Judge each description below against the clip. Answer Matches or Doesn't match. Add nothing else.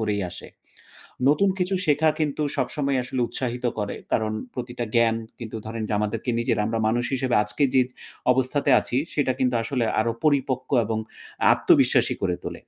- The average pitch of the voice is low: Matches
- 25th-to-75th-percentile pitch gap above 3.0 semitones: Matches